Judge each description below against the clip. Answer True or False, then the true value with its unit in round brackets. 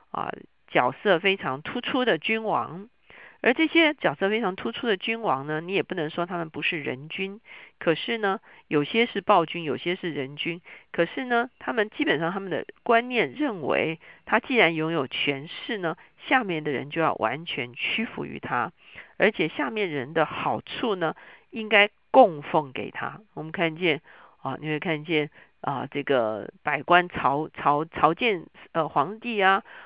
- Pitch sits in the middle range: True (180 Hz)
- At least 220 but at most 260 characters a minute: True (245 characters per minute)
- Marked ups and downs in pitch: True (6.3 semitones)